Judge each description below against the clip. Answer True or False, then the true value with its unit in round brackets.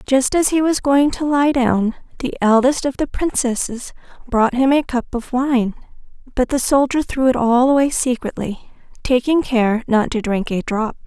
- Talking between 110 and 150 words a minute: False (185 wpm)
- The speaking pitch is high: True (255 Hz)